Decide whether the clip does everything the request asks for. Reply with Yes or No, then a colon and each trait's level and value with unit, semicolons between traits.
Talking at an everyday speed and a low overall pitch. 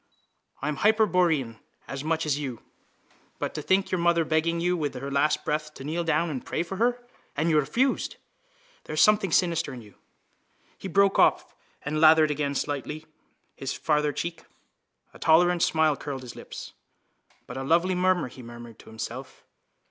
No: average, 175 wpm; medium, 155 Hz